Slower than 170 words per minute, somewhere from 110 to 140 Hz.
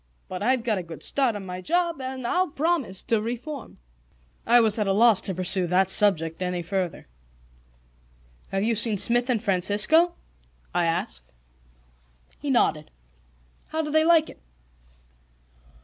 No: average, 150 wpm; high, 215 Hz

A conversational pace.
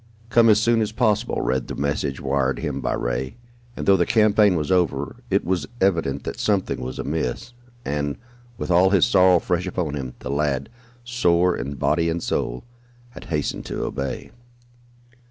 Yes: average, 175 wpm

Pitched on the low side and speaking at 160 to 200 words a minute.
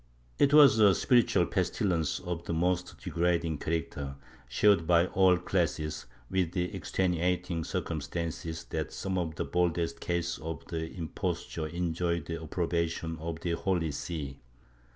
No: very low, 85 Hz; slow, 135 wpm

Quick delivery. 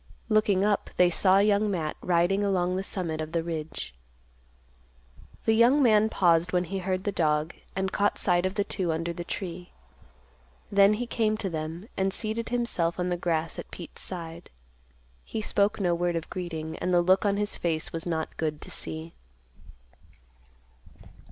No: average, 175 wpm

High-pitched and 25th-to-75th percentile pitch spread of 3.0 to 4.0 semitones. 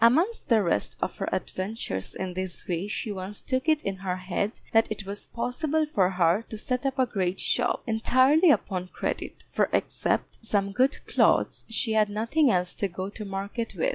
No: high, 210 Hz; average, 5.0 semitones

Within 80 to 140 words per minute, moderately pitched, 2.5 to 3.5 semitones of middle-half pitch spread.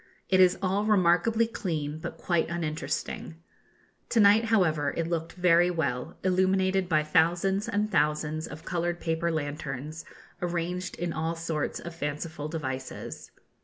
Yes: slow, 135 wpm; medium, 170 Hz; average, 3.1 semitones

